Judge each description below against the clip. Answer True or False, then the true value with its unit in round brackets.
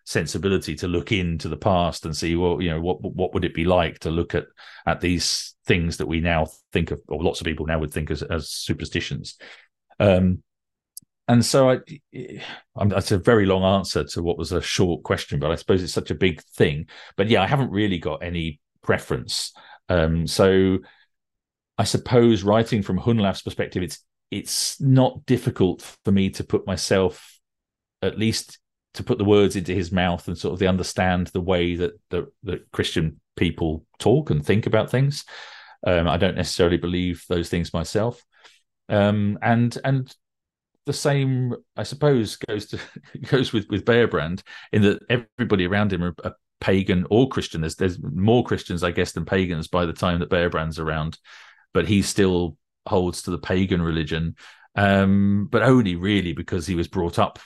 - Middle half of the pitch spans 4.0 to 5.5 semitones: False (3.5 semitones)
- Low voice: True (95 Hz)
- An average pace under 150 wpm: False (180 wpm)